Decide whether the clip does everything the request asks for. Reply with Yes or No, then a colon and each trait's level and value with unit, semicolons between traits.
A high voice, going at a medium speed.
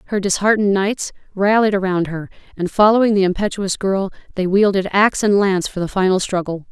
Yes: high, 195 Hz; average, 180 wpm